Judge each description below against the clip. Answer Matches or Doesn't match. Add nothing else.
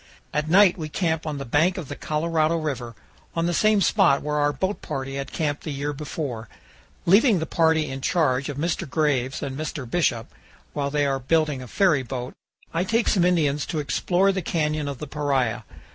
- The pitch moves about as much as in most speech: Matches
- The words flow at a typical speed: Matches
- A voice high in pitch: Doesn't match